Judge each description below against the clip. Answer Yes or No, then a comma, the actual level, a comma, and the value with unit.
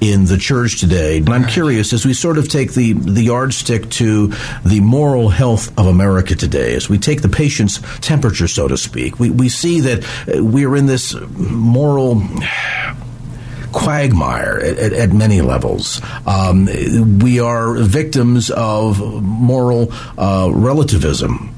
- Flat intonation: No, average, 4.0 semitones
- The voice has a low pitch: Yes, low, 115 Hz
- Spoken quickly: No, average, 150 wpm